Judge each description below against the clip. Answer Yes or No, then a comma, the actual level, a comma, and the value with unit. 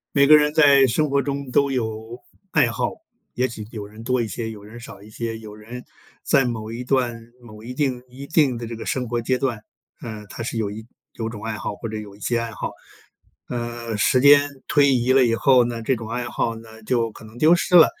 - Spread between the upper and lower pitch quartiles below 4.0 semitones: Yes, average, 2.9 semitones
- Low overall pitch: Yes, low, 120 Hz